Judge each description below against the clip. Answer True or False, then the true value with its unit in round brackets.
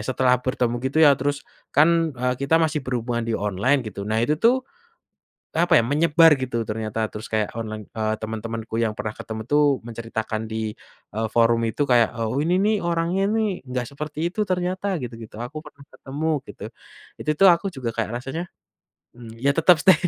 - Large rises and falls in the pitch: True (6.0 semitones)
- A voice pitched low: True (125 Hz)